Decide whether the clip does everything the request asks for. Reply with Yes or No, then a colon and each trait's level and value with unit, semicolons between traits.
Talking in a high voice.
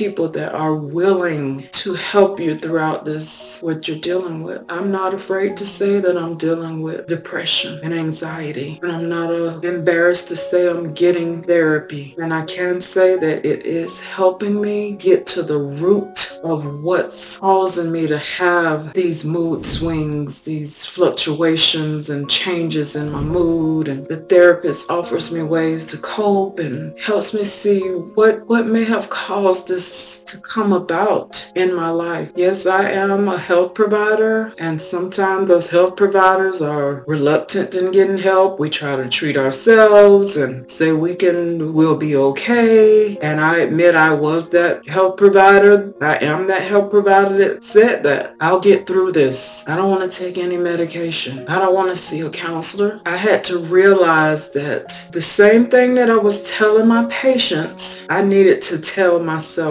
No: medium, 175 Hz